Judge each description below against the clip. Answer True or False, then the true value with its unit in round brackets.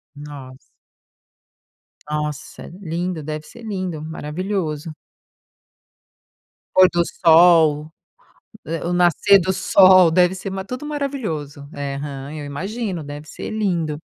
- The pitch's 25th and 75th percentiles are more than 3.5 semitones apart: True (4.0 semitones)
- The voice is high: False (165 Hz)